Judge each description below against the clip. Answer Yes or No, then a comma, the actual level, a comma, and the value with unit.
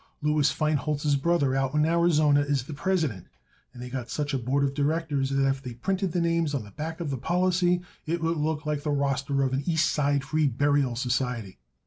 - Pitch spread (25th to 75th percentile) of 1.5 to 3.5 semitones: Yes, average, 2.9 semitones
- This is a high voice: No, medium, 145 Hz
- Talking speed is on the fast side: Yes, fast, 210 wpm